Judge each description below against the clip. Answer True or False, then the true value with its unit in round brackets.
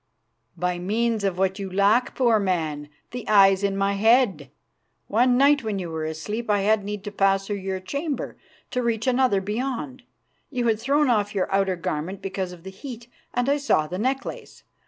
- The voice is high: True (205 Hz)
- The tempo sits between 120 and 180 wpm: False (190 wpm)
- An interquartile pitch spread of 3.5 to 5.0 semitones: True (4.0 semitones)